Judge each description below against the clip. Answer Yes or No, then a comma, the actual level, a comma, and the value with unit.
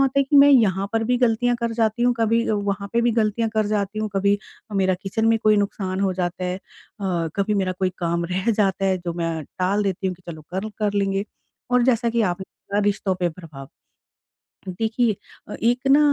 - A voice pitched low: No, high, 205 Hz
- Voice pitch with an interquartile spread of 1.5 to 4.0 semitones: Yes, average, 3.3 semitones